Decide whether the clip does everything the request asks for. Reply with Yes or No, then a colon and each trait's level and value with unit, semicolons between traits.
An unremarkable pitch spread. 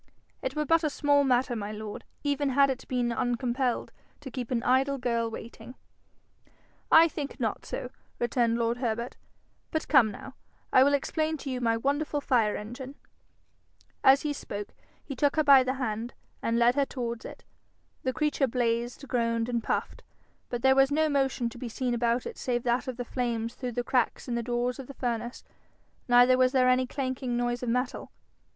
No: narrow, 2.3 semitones